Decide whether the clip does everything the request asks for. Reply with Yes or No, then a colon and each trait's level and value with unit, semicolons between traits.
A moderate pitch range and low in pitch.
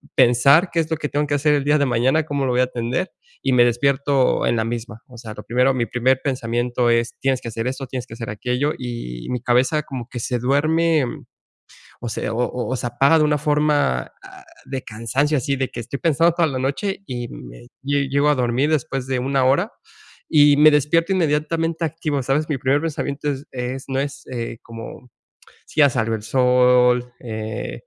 Yes: average, 3.3 semitones; low, 130 Hz